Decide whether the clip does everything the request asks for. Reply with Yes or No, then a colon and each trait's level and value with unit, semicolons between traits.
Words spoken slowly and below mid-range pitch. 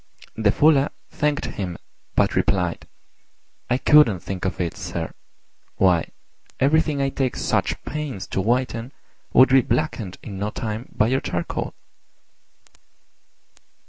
Yes: slow, 125 wpm; low, 115 Hz